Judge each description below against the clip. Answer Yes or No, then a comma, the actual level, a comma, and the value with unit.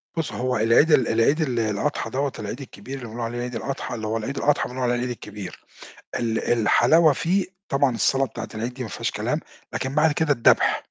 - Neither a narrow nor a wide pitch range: Yes, average, 3.6 semitones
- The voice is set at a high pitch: No, low, 125 Hz